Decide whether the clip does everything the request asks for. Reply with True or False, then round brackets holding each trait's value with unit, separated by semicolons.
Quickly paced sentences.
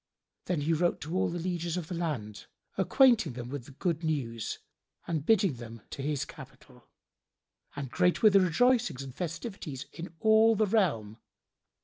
False (165 wpm)